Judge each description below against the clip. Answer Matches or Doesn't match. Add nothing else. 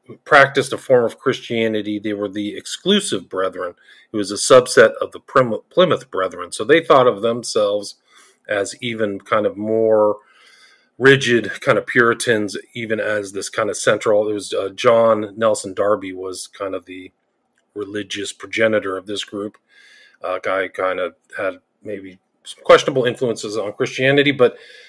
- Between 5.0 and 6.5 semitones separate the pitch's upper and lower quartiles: Matches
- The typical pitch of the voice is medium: Doesn't match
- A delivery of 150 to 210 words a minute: Matches